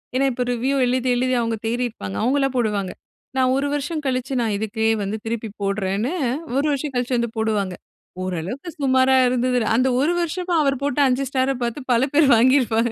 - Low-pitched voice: No, very high, 250 Hz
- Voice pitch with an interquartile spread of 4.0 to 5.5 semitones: No, average, 3.4 semitones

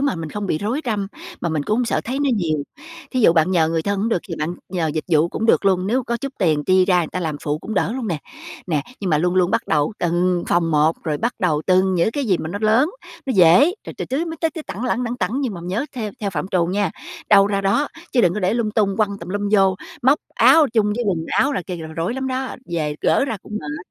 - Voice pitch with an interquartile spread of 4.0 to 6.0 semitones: Yes, wide, 5.5 semitones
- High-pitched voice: Yes, high, 195 Hz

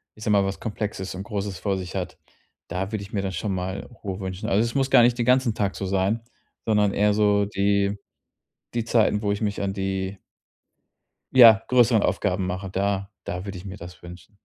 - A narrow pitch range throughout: Yes, narrow, 1.9 semitones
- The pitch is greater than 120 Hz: No, low, 100 Hz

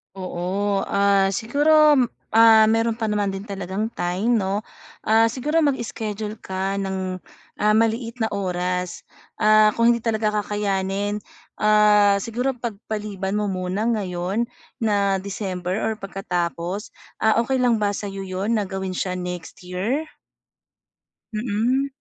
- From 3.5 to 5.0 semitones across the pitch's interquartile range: No, average, 2.8 semitones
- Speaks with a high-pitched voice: Yes, high, 205 Hz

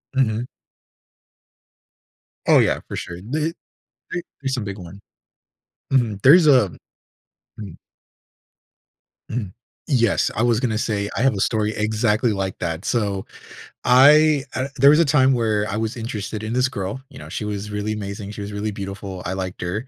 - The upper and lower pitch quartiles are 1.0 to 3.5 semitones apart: No, average, 4.2 semitones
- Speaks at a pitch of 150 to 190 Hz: No, low, 110 Hz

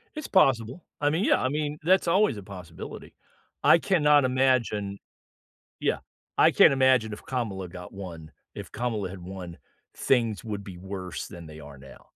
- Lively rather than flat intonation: Yes, wide, 6.6 semitones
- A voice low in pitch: Yes, low, 110 Hz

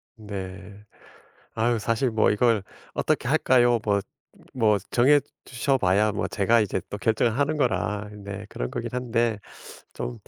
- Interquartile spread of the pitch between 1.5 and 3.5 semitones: Yes, average, 2.9 semitones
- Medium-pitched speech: No, low, 110 Hz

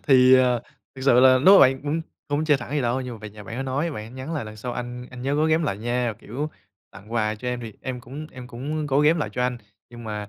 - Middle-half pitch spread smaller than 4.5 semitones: Yes, average, 3.2 semitones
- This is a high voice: No, low, 125 Hz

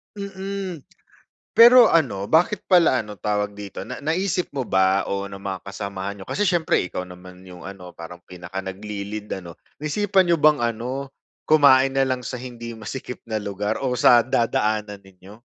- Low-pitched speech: Yes, low, 110 Hz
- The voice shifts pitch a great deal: Yes, wide, 7.4 semitones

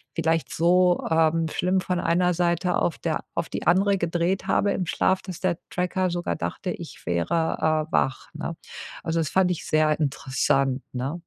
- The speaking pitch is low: No, medium, 170 Hz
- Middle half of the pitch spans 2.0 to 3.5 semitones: Yes, narrow, 2.5 semitones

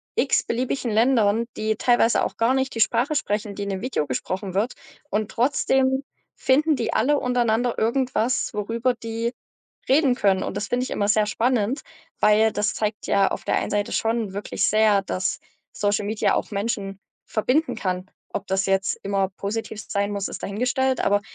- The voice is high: Yes, high, 220 Hz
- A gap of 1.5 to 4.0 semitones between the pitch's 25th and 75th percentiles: Yes, average, 3.6 semitones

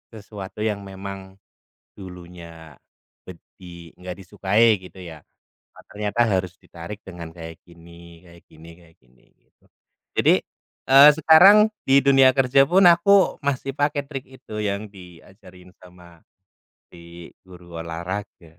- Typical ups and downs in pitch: No, wide, 5.8 semitones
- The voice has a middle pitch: No, very low, 95 Hz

